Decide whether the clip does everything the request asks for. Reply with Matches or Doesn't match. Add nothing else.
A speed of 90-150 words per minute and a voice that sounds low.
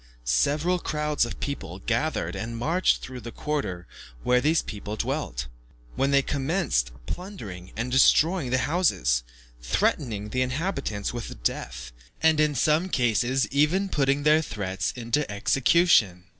Matches